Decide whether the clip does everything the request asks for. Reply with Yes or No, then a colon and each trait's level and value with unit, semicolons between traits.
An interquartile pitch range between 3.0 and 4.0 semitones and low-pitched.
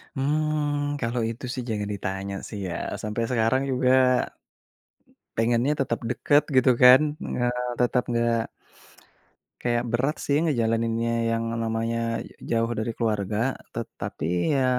No: narrow, 2.6 semitones; low, 120 Hz